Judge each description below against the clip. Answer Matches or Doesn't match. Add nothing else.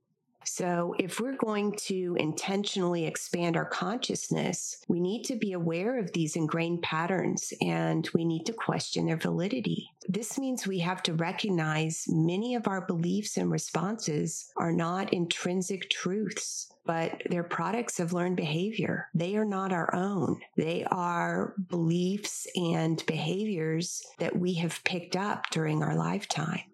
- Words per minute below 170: Matches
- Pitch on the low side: Doesn't match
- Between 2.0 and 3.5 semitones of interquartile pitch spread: Matches